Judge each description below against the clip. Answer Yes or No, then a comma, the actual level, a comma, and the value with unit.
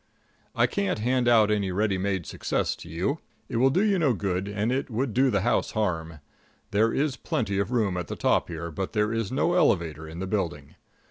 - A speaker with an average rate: No, fast, 215 wpm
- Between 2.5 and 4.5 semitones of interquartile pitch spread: No, average, 5.3 semitones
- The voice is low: Yes, low, 105 Hz